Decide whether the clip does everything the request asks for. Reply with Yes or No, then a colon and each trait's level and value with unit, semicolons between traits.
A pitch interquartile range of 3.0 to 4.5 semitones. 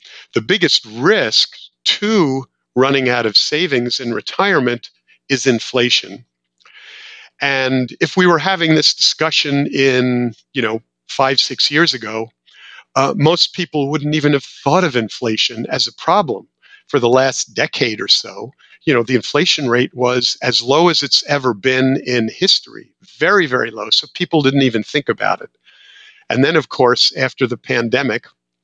Yes: average, 3.7 semitones